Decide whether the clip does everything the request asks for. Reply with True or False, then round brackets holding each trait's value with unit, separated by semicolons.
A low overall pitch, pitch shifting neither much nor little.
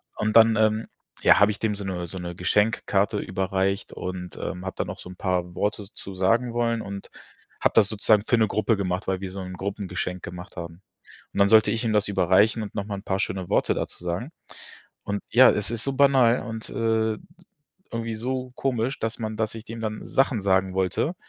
True (105 Hz; 3.1 semitones)